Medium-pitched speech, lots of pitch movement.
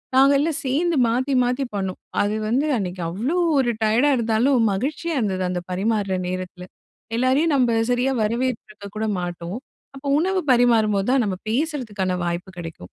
No: high, 230 Hz; wide, 5.7 semitones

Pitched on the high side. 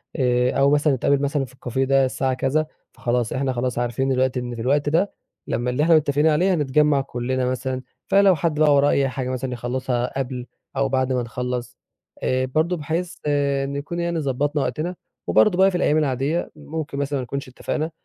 No: low, 135 Hz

